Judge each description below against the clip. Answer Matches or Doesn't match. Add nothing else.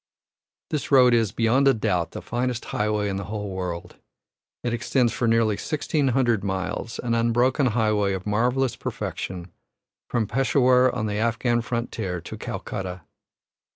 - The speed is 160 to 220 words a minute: Doesn't match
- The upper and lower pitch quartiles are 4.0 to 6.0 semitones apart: Doesn't match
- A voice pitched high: Doesn't match